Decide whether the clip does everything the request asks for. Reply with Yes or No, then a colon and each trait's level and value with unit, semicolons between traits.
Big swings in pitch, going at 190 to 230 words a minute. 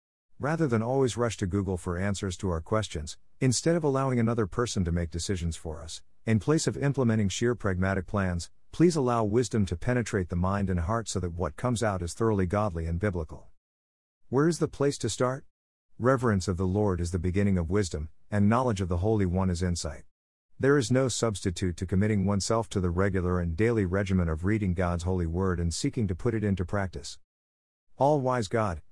No: average, 4.7 semitones; fast, 205 wpm